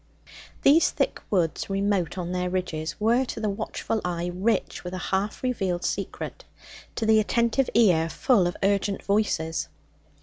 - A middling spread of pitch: Yes, average, 3.6 semitones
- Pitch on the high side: Yes, high, 195 Hz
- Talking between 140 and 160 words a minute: Yes, average, 155 wpm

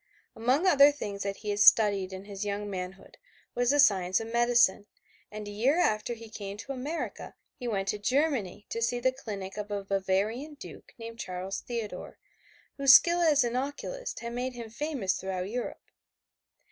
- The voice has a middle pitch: No, high, 225 Hz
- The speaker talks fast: No, average, 180 wpm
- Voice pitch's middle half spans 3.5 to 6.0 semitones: Yes, average, 4.4 semitones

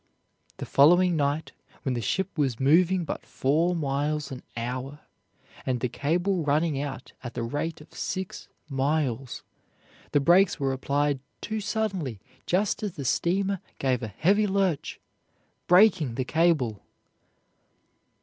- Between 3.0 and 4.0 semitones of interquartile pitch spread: No, average, 5.0 semitones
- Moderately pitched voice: Yes, medium, 150 Hz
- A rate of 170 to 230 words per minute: No, slow, 135 wpm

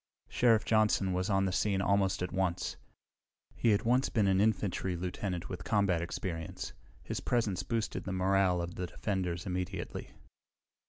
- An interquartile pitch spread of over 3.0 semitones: No, narrow, 2.5 semitones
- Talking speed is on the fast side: No, average, 155 wpm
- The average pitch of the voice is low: Yes, very low, 95 Hz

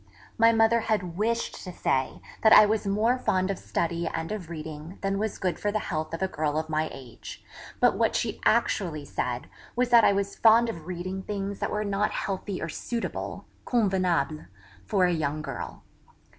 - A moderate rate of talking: Yes, average, 190 wpm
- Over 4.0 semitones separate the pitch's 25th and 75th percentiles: Yes, average, 5.0 semitones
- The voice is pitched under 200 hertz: Yes, high, 190 Hz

